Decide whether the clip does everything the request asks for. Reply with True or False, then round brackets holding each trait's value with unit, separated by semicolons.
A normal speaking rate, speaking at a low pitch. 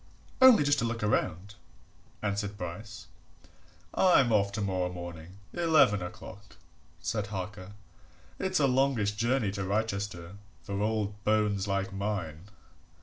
False (120 wpm; 105 Hz)